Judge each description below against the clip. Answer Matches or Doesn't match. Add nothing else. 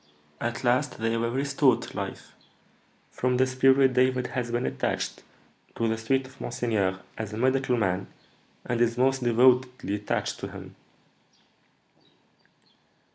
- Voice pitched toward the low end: Matches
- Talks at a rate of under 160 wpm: Matches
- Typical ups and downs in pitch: Doesn't match